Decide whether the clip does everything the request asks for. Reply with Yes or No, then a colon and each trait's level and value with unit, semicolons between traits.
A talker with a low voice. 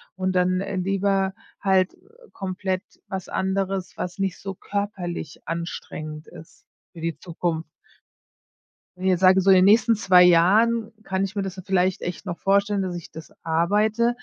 No: high, 190 Hz